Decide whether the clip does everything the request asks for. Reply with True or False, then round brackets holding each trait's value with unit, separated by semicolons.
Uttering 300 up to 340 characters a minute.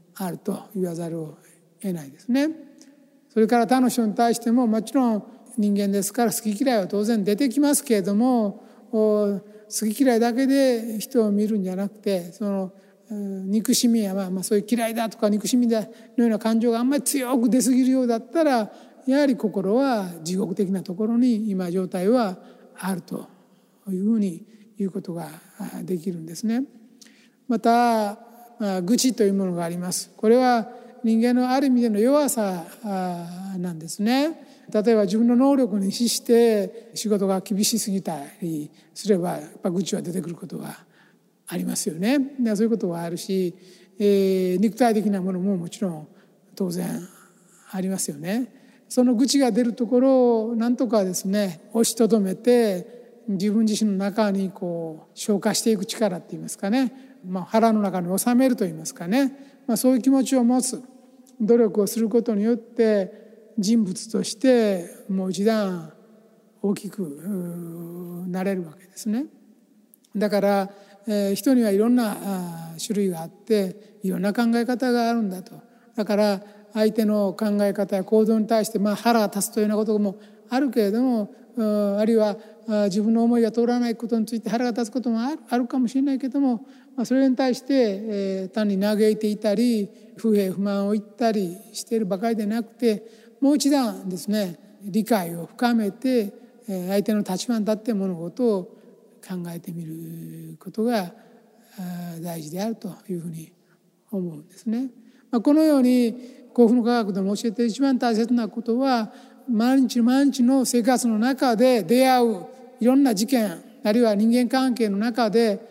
True (320 characters per minute)